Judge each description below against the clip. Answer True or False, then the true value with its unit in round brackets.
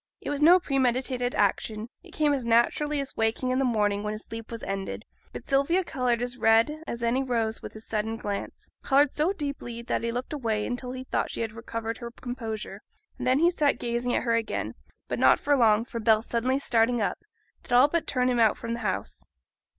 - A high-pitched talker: True (240 Hz)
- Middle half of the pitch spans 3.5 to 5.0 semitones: False (3.1 semitones)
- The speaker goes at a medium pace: False (220 wpm)